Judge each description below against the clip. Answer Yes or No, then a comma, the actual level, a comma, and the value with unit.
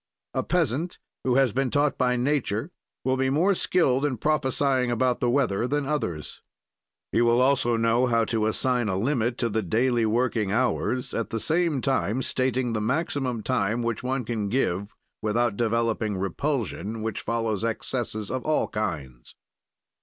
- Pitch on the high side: No, low, 120 Hz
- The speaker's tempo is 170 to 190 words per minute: No, average, 160 wpm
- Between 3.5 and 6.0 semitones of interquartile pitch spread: No, average, 3.1 semitones